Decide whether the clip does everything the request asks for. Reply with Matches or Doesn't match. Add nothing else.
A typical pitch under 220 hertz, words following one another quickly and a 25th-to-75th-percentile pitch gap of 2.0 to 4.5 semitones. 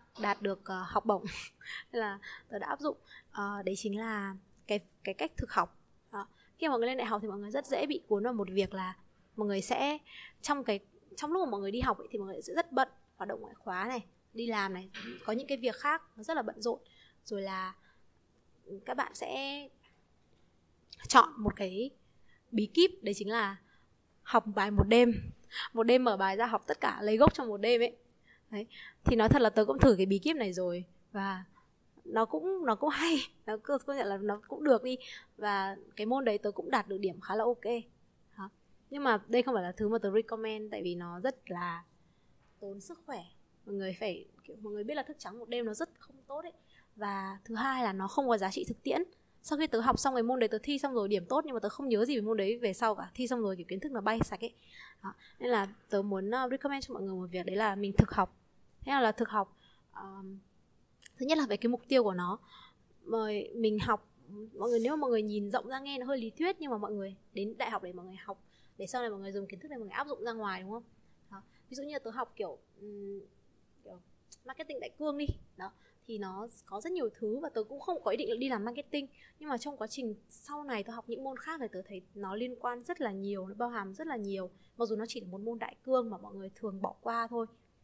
Doesn't match